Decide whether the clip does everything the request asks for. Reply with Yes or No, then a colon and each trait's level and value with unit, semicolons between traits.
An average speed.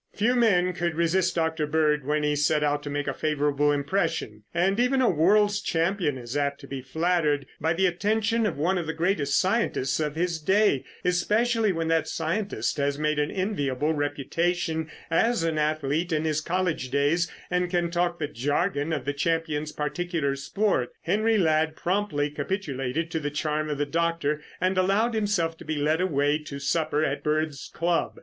Yes: average, 180 wpm